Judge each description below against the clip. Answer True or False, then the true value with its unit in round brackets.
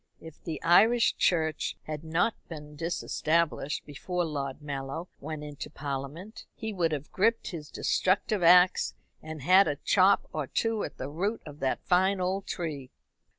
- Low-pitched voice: False (165 Hz)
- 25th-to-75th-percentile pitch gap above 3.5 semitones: True (4.0 semitones)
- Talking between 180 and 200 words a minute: False (155 wpm)